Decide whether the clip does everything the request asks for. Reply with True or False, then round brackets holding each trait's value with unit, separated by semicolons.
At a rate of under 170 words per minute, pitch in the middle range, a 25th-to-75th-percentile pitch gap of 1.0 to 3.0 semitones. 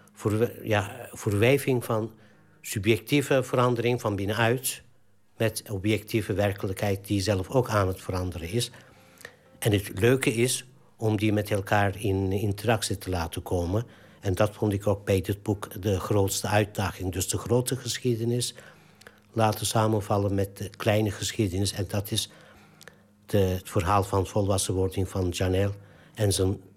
False (140 wpm; 105 Hz; 2.5 semitones)